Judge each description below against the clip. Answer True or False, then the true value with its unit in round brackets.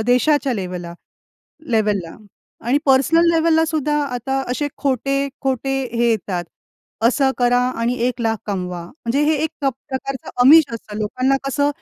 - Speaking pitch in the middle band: False (260 Hz)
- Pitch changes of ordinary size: True (3.8 semitones)